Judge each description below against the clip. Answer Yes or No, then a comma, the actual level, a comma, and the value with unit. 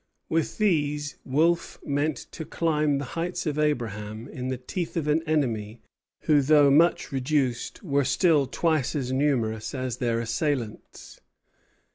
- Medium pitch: Yes, medium, 145 Hz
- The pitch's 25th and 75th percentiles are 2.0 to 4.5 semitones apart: Yes, average, 3.7 semitones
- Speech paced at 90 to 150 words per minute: Yes, average, 140 wpm